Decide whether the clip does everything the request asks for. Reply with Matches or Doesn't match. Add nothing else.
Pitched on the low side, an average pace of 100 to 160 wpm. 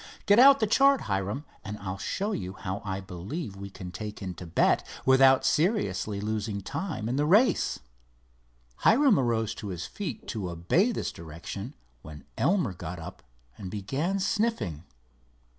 Matches